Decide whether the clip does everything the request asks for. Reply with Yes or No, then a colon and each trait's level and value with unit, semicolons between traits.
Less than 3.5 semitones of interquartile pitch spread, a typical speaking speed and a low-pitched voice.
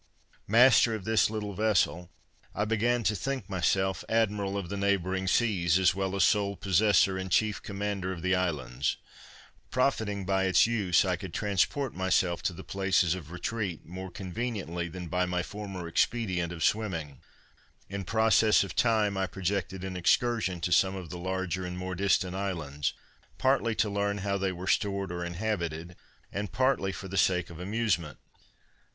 Yes: narrow, 2.6 semitones; average, 170 wpm; very low, 95 Hz